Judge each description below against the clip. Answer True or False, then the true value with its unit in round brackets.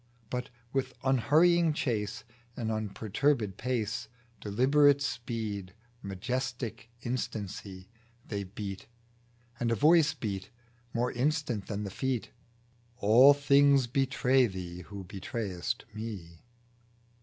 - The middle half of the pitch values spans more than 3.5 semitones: True (4.8 semitones)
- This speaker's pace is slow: True (105 wpm)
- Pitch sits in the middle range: False (115 Hz)